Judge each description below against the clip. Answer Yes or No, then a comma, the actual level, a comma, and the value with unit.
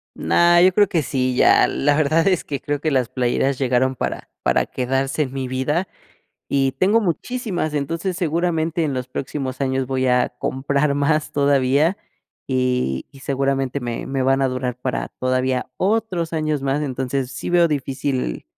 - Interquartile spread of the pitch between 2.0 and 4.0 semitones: Yes, average, 3.5 semitones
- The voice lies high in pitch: No, medium, 140 Hz